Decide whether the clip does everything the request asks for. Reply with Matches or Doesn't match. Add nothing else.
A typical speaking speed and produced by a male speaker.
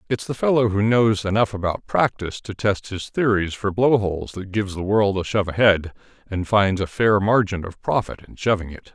Doesn't match